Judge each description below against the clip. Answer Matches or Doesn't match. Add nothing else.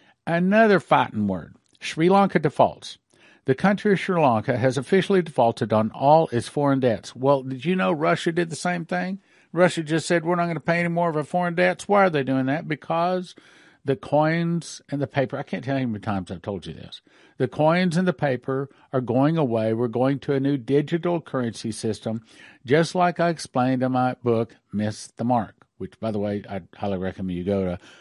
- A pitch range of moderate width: Doesn't match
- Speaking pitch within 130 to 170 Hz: Matches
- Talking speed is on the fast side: Matches